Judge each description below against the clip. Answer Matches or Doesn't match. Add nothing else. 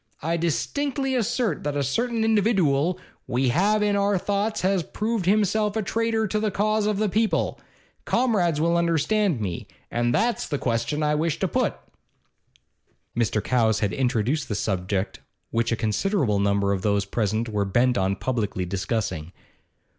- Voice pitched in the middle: Matches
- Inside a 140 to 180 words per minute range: Matches